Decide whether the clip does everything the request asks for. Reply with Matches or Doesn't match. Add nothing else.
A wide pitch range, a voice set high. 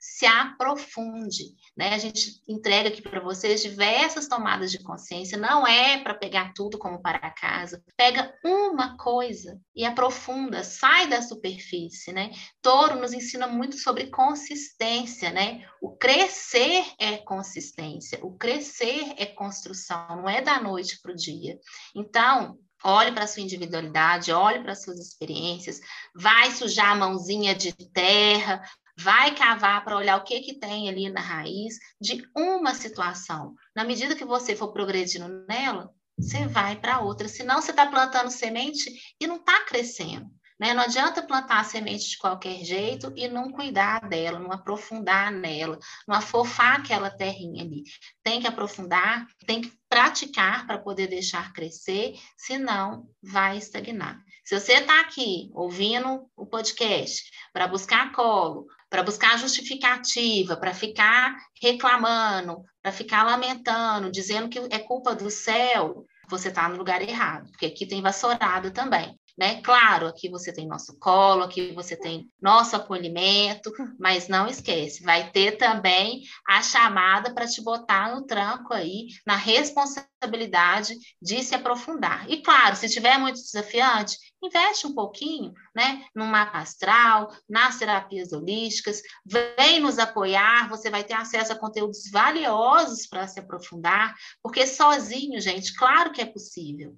Doesn't match